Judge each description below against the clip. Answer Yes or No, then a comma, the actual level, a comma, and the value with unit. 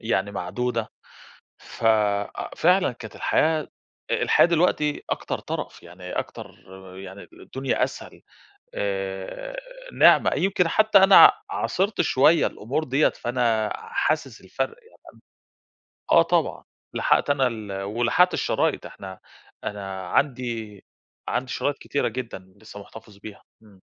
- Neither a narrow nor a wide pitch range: No, wide, 7.6 semitones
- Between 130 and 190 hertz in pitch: No, low, 120 Hz